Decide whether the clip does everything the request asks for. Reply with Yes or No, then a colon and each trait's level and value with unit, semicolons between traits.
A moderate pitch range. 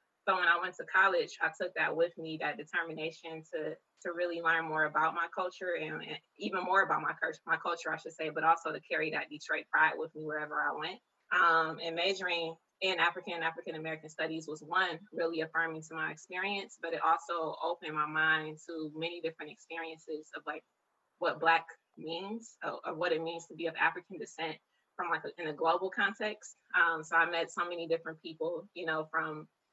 No: narrow, 1.4 semitones